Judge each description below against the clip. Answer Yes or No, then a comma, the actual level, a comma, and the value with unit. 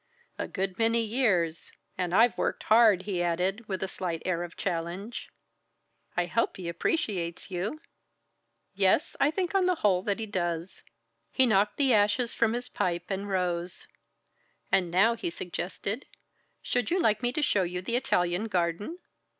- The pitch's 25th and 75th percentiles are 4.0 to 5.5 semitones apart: Yes, average, 4.6 semitones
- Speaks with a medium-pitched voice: No, high, 195 Hz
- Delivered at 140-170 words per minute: Yes, average, 165 wpm